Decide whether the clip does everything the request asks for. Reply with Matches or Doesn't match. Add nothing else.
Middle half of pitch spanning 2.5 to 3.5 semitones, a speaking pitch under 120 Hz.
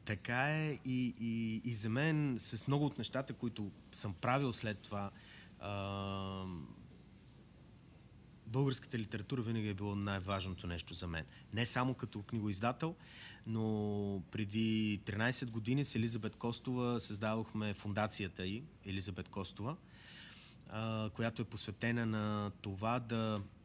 Matches